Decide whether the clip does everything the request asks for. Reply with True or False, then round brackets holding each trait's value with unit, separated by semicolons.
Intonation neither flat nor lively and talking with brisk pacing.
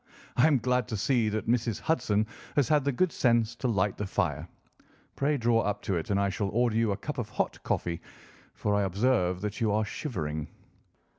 True (3.8 semitones; 215 wpm)